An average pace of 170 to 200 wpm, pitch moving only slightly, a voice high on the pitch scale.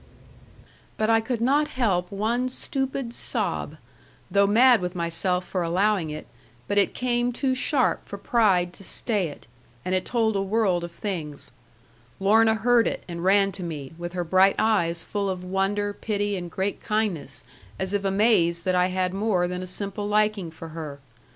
No: average, 175 wpm; average, 3.6 semitones; high, 195 Hz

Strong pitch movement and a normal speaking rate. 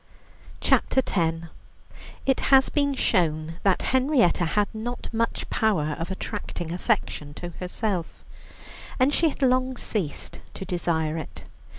No: wide, 7.4 semitones; slow, 125 wpm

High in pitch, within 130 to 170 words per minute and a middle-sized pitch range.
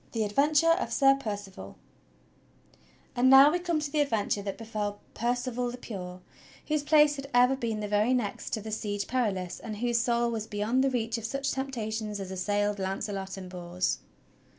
No: high, 225 Hz; average, 180 wpm; average, 4.3 semitones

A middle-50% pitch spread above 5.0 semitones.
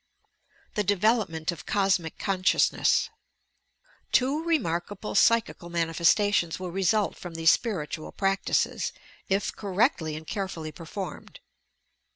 No: average, 3.8 semitones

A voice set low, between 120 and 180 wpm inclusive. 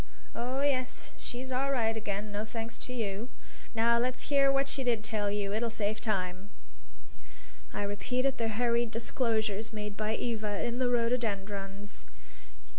No: high, 225 Hz; average, 150 wpm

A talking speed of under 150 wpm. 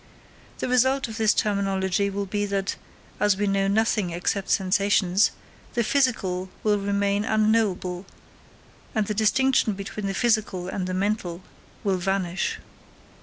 Yes: slow, 135 wpm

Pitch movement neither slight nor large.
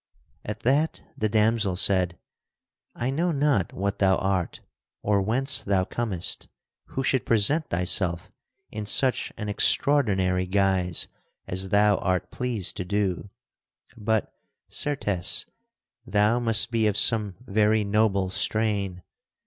Yes: average, 3.4 semitones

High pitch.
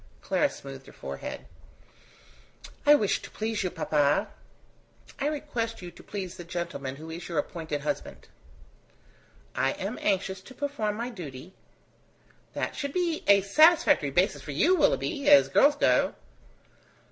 Yes: high, 200 Hz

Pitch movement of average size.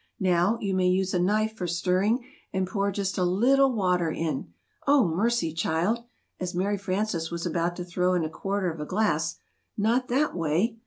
Yes: average, 3.6 semitones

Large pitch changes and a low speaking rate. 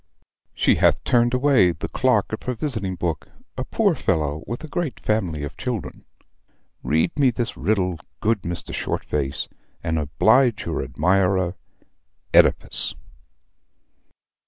Yes: wide, 6.6 semitones; slow, 130 wpm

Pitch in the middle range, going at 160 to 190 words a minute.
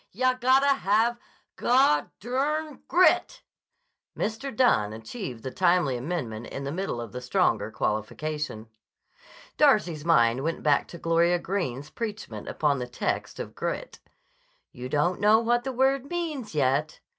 No: medium, 175 Hz; slow, 135 wpm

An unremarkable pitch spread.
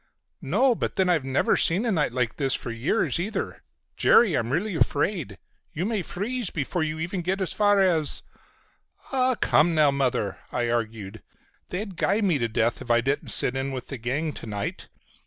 No: wide, 7.5 semitones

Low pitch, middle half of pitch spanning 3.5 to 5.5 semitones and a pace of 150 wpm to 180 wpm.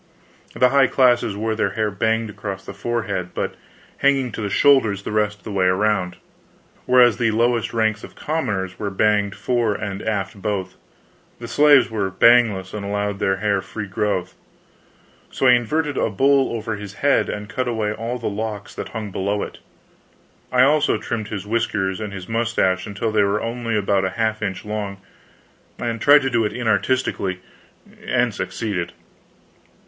No: low, 110 Hz; average, 2.9 semitones; average, 170 wpm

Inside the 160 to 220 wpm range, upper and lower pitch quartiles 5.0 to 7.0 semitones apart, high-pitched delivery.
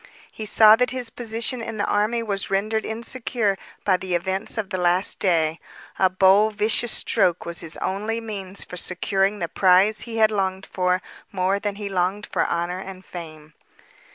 No: average, 175 wpm; average, 3.0 semitones; high, 195 Hz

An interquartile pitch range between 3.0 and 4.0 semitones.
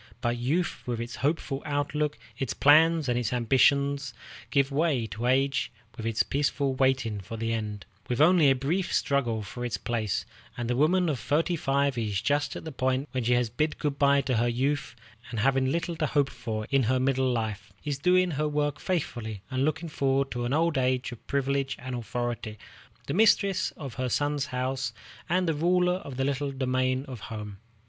Yes: average, 3.4 semitones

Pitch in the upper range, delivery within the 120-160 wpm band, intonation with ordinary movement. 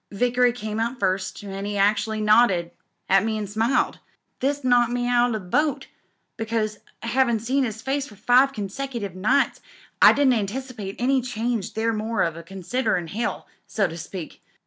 No: high, 225 Hz; average, 175 wpm; average, 3.6 semitones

